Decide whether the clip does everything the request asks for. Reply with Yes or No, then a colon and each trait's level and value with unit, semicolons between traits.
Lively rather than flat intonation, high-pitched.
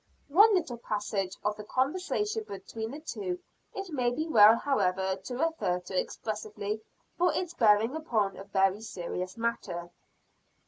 Yes: wide, 8.1 semitones; high, 225 Hz